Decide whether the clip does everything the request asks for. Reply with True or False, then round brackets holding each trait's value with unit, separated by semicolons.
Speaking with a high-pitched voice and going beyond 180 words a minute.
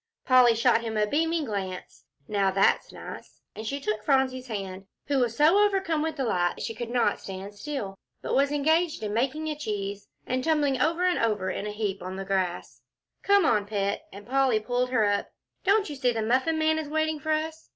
True (250 Hz; 200 wpm)